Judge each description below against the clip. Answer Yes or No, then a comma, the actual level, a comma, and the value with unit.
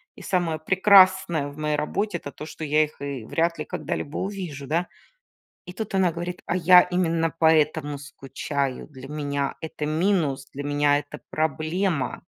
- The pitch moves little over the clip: No, average, 3.7 semitones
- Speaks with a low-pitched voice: No, medium, 155 Hz